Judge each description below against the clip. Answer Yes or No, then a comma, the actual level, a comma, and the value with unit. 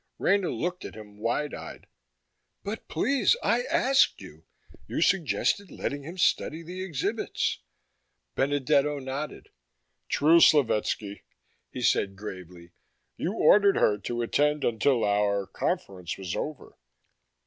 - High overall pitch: No, medium, 145 Hz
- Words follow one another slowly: Yes, slow, 120 wpm